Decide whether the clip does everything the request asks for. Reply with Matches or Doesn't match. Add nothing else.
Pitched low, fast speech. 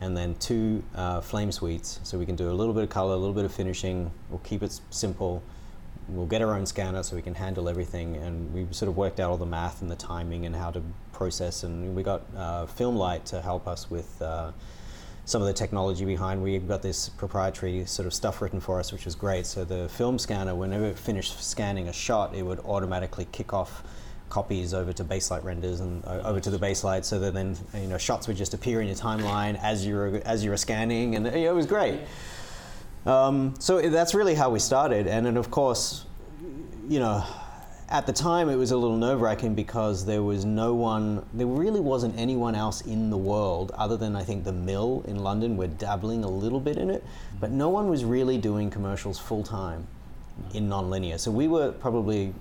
Matches